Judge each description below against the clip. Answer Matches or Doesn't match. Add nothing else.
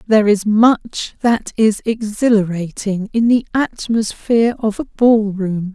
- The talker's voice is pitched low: Doesn't match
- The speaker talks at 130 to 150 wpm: Matches